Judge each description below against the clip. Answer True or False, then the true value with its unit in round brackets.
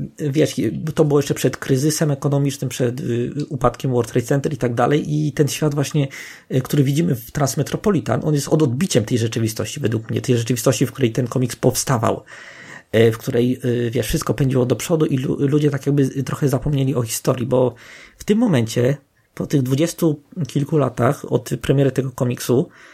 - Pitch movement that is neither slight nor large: True (3.3 semitones)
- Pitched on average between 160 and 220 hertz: False (135 Hz)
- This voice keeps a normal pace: False (175 wpm)